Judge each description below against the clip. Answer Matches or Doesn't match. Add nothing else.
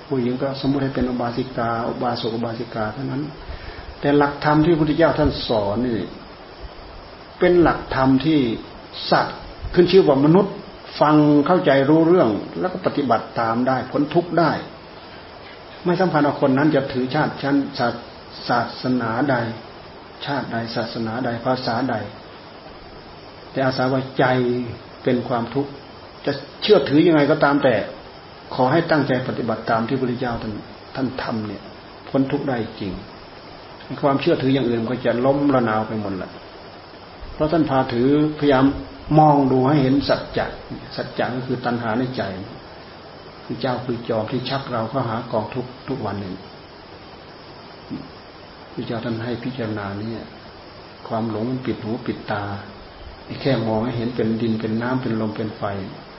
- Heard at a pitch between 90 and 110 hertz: Doesn't match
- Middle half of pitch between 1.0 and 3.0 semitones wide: Doesn't match